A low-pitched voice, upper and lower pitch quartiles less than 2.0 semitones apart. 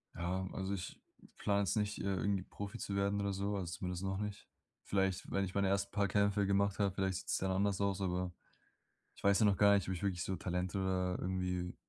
Yes: very low, 95 Hz; narrow, 1.5 semitones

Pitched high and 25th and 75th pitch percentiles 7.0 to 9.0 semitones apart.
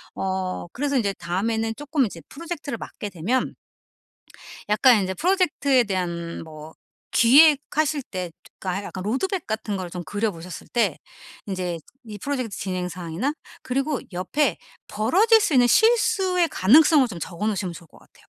Yes: high, 220 Hz; wide, 7.8 semitones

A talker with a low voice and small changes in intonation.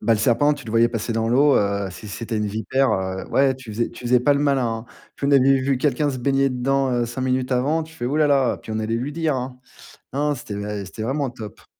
No: low, 125 Hz; average, 3.4 semitones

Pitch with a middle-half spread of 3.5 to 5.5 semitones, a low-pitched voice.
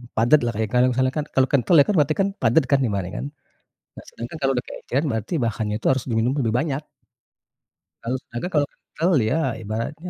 Yes: average, 4.5 semitones; low, 130 Hz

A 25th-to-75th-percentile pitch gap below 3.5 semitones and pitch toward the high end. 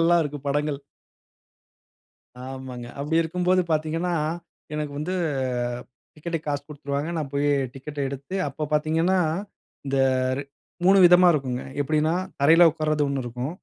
No: average, 2.8 semitones; medium, 150 Hz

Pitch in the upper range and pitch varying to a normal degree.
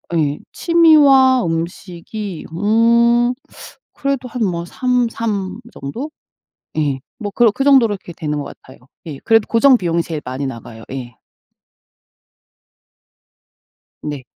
No: high, 205 Hz; wide, 7.9 semitones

